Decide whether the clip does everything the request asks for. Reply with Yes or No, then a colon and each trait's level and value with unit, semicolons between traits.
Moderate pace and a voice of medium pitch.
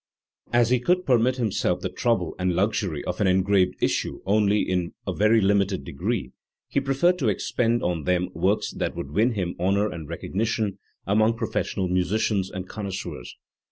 No: average, 170 wpm; low, 100 Hz